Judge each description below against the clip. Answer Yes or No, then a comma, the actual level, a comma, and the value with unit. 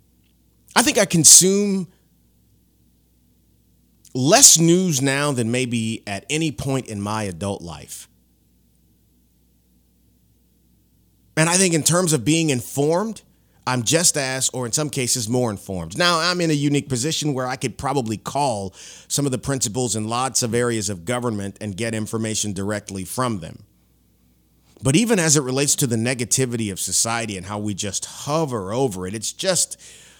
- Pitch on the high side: No, low, 120 Hz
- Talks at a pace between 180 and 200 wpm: No, average, 155 wpm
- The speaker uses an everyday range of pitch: No, wide, 7.1 semitones